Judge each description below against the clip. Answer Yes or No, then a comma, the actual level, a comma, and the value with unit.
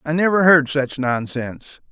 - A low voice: No, medium, 145 Hz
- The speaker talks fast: No, average, 155 wpm